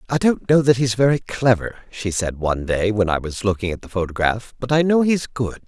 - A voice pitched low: Yes, low, 115 Hz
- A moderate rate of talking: No, fast, 245 wpm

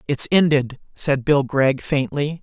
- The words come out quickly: No, average, 150 wpm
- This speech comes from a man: Yes, male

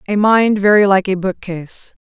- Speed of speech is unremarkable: Yes, average, 175 wpm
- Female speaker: Yes, female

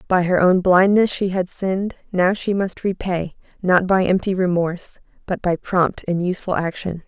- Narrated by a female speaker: Yes, female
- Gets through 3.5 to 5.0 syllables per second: Yes, 4.8 syllables/s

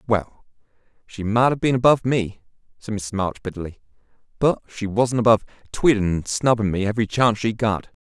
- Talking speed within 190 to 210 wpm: No, average, 170 wpm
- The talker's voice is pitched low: Yes, low, 110 Hz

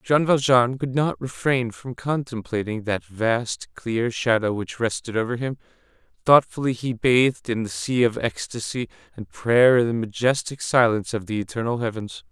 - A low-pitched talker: Yes, low, 120 Hz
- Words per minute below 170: Yes, average, 160 wpm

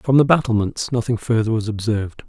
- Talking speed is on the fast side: No, average, 185 wpm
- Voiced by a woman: No, male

